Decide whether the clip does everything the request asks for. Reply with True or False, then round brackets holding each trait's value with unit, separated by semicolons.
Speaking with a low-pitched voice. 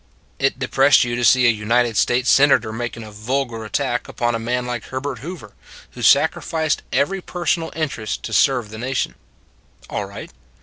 True (125 Hz)